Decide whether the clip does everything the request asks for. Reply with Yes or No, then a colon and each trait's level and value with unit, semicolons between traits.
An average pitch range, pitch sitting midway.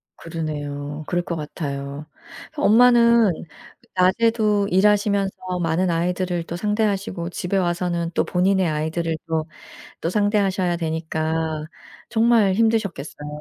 Yes: average, 4.2 semitones; medium, 180 Hz